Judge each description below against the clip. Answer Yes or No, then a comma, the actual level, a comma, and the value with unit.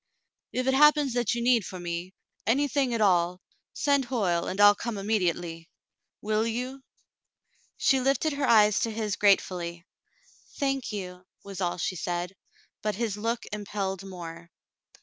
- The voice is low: No, high, 210 Hz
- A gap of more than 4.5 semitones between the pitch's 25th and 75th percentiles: Yes, average, 5.3 semitones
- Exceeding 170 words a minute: No, average, 155 wpm